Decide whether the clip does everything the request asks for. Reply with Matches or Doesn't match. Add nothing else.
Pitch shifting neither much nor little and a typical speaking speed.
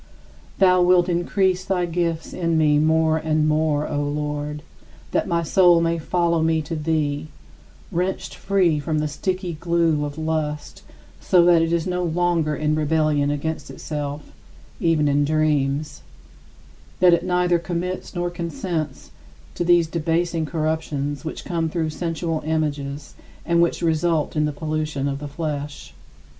Doesn't match